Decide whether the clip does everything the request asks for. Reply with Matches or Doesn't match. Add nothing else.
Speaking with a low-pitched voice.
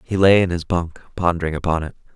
Matches